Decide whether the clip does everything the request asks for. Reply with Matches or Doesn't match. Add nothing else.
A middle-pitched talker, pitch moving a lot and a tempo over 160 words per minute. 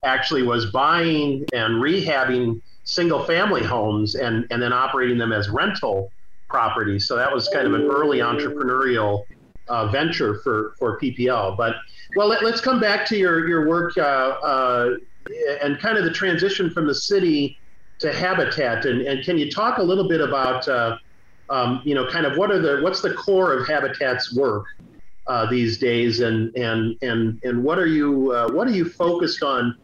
Doesn't match